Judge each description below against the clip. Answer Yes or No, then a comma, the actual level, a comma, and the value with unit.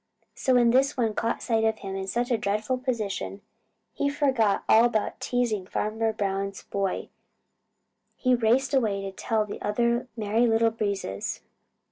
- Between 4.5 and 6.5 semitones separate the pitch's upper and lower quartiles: No, average, 3.1 semitones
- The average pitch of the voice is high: Yes, high, 225 Hz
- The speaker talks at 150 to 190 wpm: Yes, average, 155 wpm